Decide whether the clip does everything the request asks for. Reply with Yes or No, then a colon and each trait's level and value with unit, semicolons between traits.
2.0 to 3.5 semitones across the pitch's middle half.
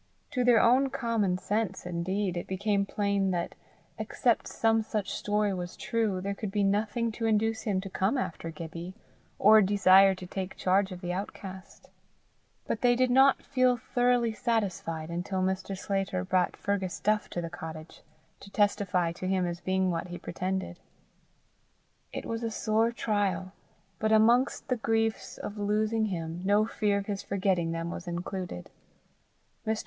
Yes: average, 3.1 semitones